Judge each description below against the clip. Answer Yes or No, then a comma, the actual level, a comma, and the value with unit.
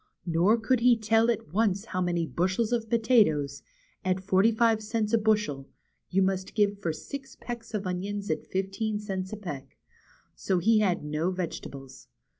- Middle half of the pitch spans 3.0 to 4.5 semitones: Yes, average, 3.7 semitones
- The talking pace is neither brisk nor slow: Yes, average, 170 wpm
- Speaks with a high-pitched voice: Yes, high, 200 Hz